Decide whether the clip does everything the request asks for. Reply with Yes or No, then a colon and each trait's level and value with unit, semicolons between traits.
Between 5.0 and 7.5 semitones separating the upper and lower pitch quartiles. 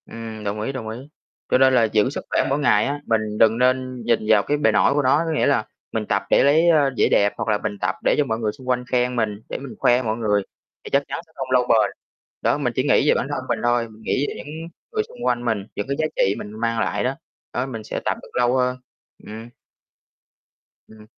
No: average, 3.5 semitones